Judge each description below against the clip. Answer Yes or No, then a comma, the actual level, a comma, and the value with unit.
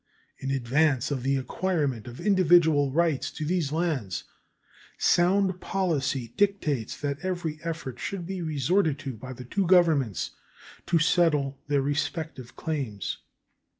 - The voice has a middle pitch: Yes, medium, 150 Hz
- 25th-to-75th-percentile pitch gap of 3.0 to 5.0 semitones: Yes, average, 4.6 semitones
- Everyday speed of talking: No, slow, 130 wpm